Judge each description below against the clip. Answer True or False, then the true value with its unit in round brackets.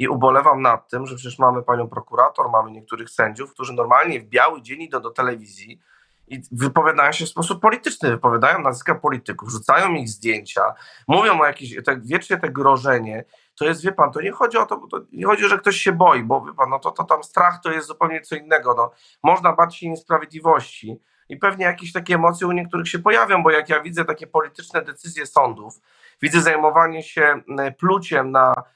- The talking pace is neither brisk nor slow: False (200 wpm)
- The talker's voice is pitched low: False (160 Hz)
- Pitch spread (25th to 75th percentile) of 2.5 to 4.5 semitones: False (5.1 semitones)